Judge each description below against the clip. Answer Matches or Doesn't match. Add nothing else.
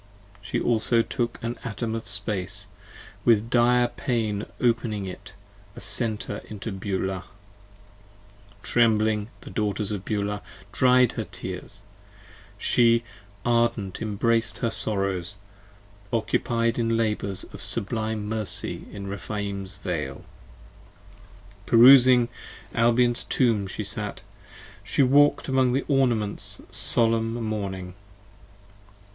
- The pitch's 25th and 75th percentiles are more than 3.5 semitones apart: Doesn't match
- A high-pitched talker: Doesn't match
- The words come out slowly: Matches